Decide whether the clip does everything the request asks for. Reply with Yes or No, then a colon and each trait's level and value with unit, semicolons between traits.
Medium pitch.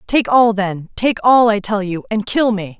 No: high, 215 Hz